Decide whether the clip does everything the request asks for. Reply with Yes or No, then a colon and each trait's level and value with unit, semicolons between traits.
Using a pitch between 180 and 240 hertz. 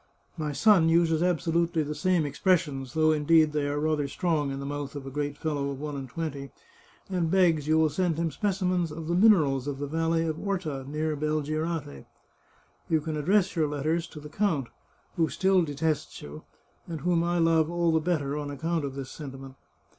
No: medium, 155 Hz